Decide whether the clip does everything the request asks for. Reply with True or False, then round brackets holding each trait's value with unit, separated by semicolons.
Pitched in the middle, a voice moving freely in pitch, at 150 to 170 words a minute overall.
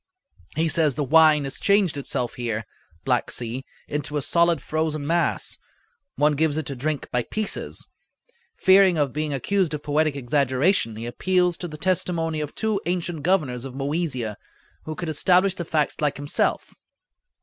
False (155 Hz; 3.8 semitones; 160 wpm)